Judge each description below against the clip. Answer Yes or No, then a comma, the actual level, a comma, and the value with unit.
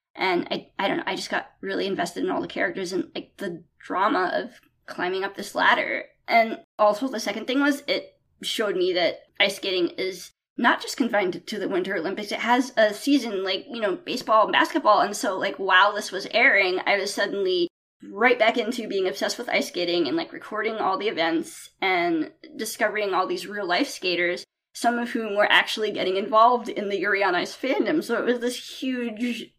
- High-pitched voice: Yes, high, 230 Hz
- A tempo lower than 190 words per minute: No, fast, 205 wpm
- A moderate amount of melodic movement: No, wide, 7.1 semitones